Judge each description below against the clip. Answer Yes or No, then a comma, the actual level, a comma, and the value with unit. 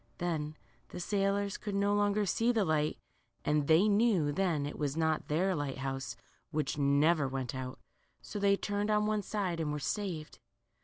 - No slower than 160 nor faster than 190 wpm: Yes, average, 175 wpm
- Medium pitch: Yes, medium, 170 Hz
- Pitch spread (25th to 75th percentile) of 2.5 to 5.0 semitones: No, wide, 5.4 semitones